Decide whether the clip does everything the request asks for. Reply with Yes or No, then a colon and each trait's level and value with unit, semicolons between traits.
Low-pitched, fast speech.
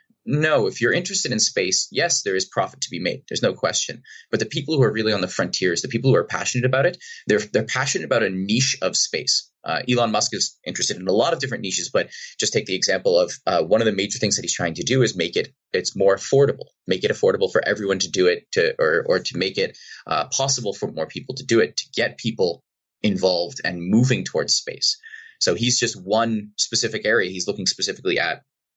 Yes: low, 130 Hz; fast, 240 wpm